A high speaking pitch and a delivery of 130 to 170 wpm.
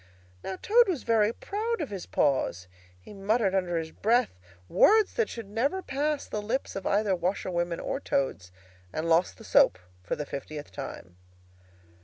Yes: high, 200 Hz; average, 165 wpm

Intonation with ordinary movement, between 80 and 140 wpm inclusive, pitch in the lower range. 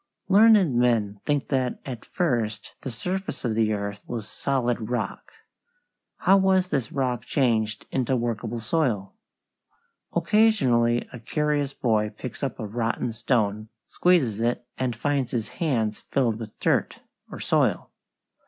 Yes: average, 4.1 semitones; slow, 135 wpm; low, 120 Hz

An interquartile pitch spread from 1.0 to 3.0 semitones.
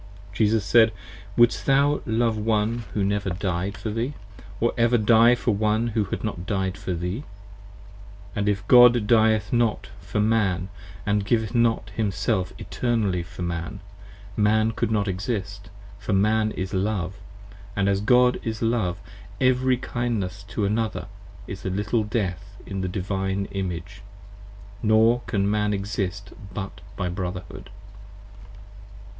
Yes: average, 2.7 semitones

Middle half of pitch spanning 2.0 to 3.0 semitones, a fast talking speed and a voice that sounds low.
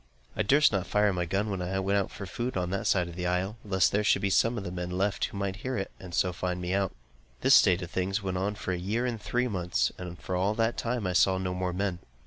Yes: narrow, 2.4 semitones; fast, 280 wpm; very low, 95 Hz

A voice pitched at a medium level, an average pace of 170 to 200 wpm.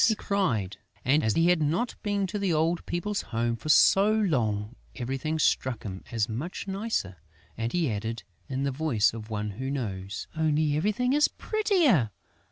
Yes: medium, 150 Hz; average, 175 wpm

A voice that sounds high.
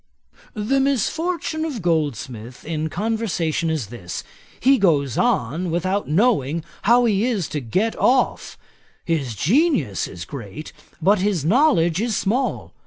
No: medium, 180 Hz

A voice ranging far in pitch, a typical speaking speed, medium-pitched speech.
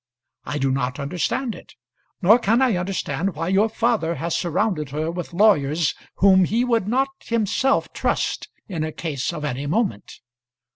Yes: wide, 6.4 semitones; average, 160 wpm; medium, 180 Hz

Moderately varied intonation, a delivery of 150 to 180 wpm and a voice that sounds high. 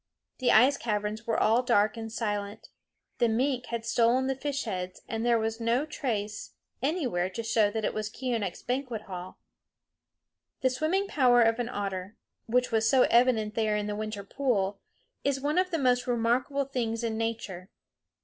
Yes: average, 3.1 semitones; average, 175 wpm; high, 230 Hz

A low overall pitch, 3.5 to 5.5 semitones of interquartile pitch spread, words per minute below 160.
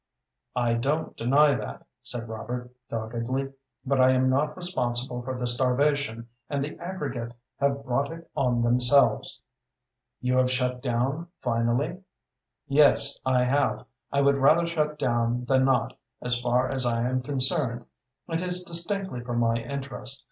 No: low, 130 Hz; average, 2.7 semitones; average, 150 wpm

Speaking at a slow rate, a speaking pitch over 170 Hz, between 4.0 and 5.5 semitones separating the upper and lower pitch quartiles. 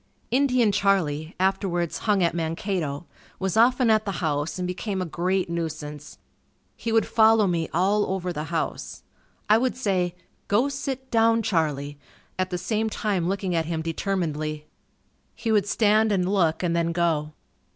No: average, 160 wpm; medium, 185 Hz; average, 4.5 semitones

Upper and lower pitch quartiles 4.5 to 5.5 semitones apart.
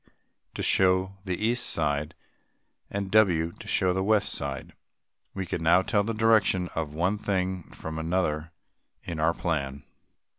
No: average, 3.5 semitones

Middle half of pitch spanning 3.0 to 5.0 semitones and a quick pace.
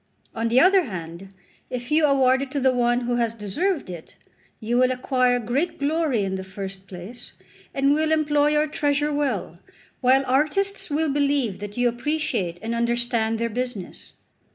No: average, 4.4 semitones; average, 170 wpm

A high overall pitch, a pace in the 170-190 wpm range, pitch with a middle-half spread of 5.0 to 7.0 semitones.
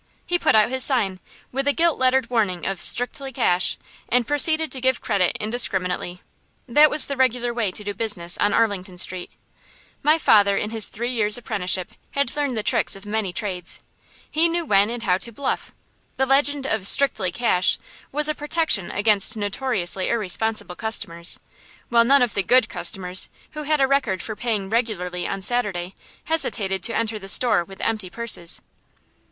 Yes: high, 220 Hz; average, 175 wpm; average, 5.3 semitones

